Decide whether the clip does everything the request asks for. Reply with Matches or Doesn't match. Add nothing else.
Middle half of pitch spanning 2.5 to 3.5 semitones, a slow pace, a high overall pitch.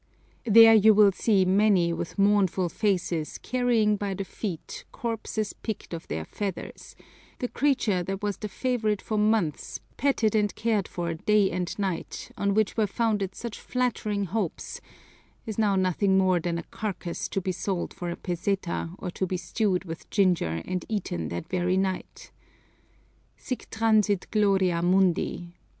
Doesn't match